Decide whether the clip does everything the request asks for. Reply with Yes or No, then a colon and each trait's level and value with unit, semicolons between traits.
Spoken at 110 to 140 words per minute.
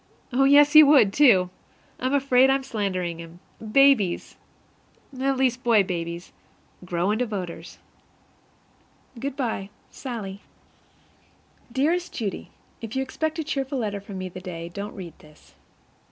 Yes: slow, 135 wpm